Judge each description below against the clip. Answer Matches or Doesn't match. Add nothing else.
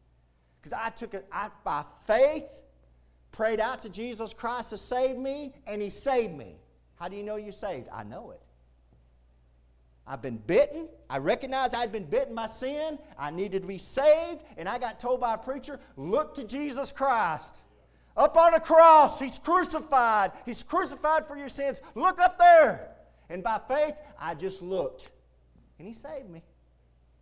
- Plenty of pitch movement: Matches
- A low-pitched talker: Doesn't match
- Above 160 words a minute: Matches